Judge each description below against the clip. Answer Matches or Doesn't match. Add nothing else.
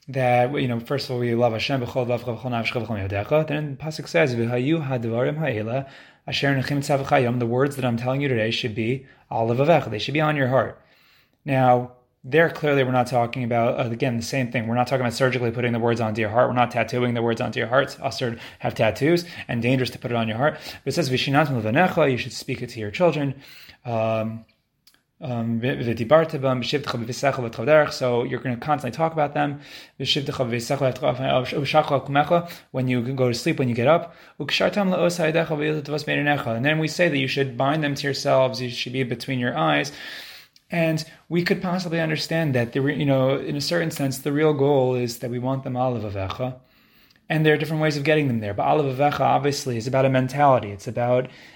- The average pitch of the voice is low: Matches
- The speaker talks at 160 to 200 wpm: Matches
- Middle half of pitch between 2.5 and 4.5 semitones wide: Matches